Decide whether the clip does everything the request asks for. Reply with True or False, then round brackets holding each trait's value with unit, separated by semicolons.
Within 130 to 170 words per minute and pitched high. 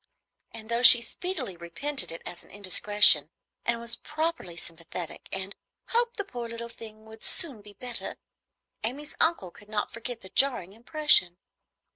True (155 wpm; 230 Hz)